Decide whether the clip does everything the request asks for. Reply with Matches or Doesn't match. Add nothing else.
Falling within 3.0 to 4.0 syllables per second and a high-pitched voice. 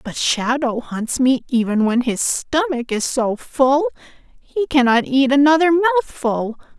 Matches